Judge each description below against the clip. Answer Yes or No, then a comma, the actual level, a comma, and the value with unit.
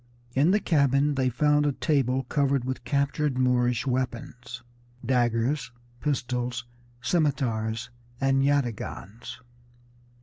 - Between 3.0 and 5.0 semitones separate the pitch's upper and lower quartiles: No, narrow, 2.6 semitones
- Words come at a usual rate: No, slow, 100 wpm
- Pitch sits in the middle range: No, low, 130 Hz